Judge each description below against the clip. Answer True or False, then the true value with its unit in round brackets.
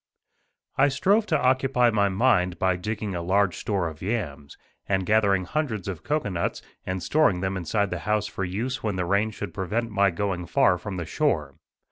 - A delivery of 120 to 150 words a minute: False (190 wpm)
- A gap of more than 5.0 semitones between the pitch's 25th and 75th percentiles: False (4.2 semitones)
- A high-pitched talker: False (100 Hz)